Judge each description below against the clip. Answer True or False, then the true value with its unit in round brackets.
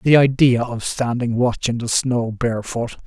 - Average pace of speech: True (175 wpm)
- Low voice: True (120 Hz)